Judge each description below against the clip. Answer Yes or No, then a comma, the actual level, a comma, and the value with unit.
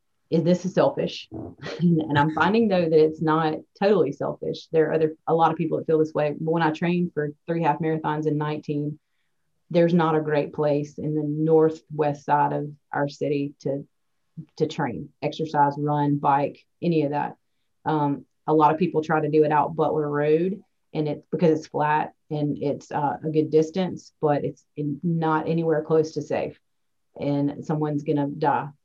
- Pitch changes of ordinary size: No, narrow, 1.5 semitones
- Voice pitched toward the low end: No, medium, 155 Hz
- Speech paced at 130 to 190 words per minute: Yes, average, 185 wpm